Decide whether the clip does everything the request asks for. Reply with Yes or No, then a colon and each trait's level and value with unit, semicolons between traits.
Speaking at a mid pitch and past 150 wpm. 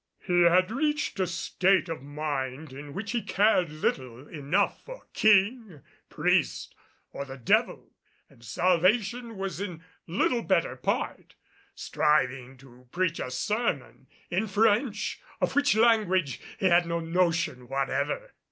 No: medium, 175 Hz; slow, 135 wpm